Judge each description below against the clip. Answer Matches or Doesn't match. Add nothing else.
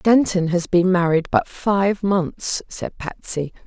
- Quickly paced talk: Doesn't match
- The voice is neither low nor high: Matches